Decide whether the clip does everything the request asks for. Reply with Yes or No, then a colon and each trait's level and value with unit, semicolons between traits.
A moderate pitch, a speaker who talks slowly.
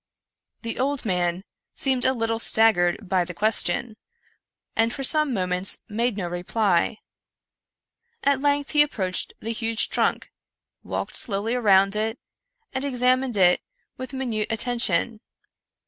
No: high, 225 Hz; slow, 130 wpm